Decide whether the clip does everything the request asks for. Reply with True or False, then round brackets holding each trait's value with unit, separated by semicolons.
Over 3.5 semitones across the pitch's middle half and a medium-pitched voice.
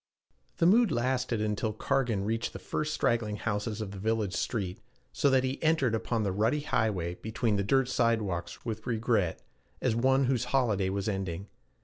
False (4.0 semitones; 110 Hz)